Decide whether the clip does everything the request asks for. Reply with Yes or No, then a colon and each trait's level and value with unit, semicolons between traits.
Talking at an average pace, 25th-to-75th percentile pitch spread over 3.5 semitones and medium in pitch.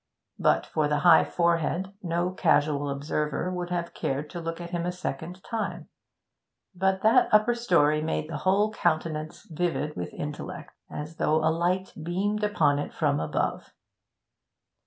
No: average, 155 wpm; average, 3.2 semitones; medium, 170 Hz